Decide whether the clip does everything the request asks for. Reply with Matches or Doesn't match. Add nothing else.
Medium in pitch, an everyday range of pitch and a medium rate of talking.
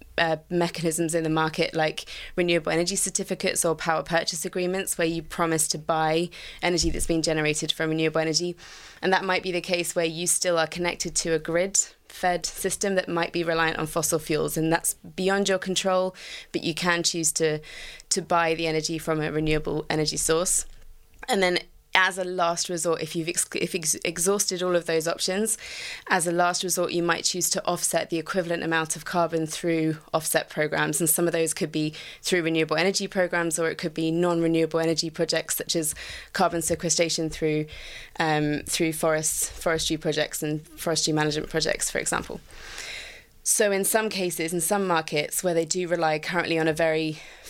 Doesn't match